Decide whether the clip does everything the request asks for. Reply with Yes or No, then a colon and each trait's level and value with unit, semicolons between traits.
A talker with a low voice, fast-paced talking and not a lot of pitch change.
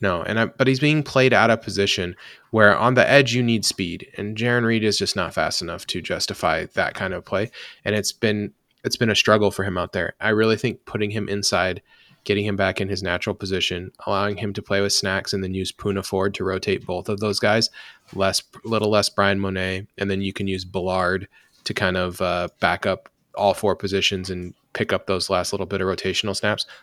Yes: low, 100 Hz; fast, 230 wpm; narrow, 1.9 semitones